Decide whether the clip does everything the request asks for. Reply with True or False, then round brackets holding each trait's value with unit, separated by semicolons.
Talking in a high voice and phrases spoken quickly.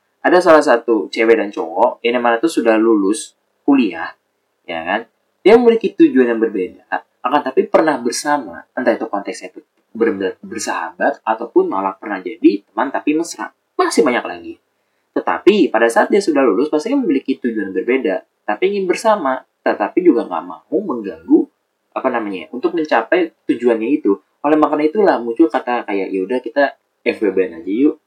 True (220 Hz; 160 wpm)